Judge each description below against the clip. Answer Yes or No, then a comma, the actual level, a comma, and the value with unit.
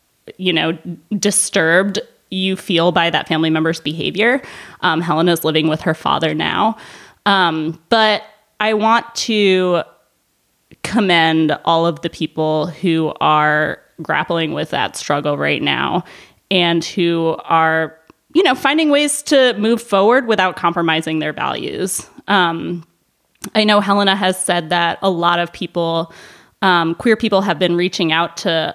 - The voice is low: No, medium, 175 Hz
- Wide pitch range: No, average, 4.1 semitones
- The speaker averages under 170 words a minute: Yes, average, 140 wpm